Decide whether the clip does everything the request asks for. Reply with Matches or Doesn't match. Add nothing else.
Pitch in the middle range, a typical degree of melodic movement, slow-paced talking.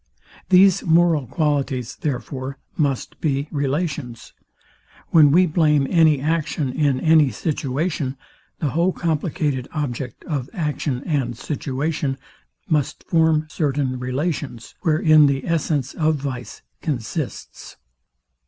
Matches